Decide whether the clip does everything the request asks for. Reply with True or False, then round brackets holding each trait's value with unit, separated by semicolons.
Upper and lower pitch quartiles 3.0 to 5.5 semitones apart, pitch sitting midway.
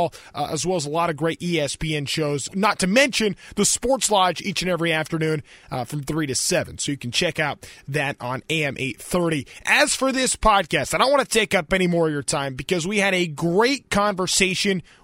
True (4.7 semitones; 170 Hz)